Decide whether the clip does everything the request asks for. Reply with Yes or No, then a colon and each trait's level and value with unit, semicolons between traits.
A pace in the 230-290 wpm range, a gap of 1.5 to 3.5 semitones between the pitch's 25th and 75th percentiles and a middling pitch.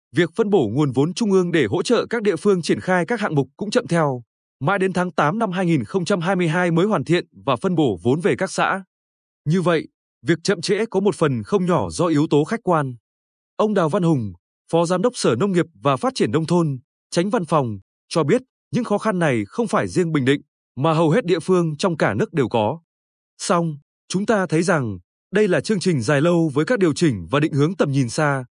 No: average, 235 wpm; average, 5.1 semitones; medium, 170 Hz